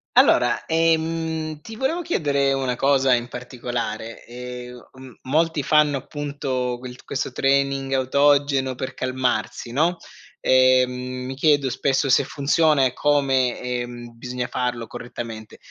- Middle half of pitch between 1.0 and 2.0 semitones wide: No, narrow, 2.6 semitones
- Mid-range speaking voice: No, low, 130 Hz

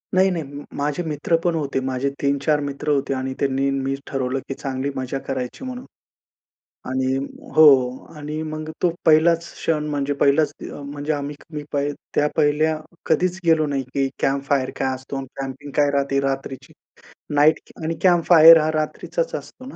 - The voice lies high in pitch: No, medium, 145 Hz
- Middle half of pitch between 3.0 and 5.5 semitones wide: No, narrow, 2.5 semitones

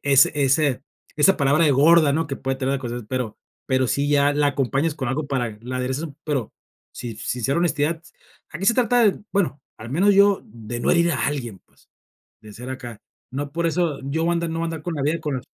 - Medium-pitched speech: Yes, medium, 145 Hz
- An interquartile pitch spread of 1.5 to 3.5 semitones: No, average, 4.0 semitones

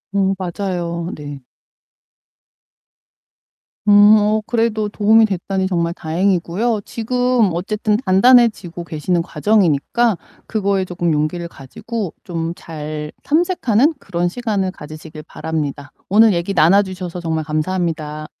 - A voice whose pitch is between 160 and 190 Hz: Yes, medium, 185 Hz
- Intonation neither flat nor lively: Yes, average, 4.5 semitones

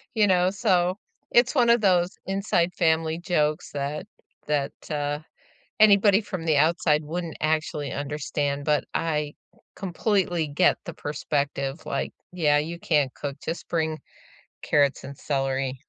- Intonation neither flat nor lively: Yes, average, 3.5 semitones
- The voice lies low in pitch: No, medium, 160 Hz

